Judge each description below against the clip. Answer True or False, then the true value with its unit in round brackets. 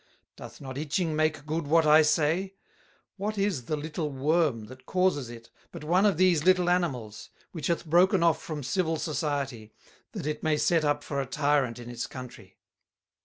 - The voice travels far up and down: False (3.9 semitones)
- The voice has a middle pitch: True (155 Hz)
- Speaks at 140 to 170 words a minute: False (180 wpm)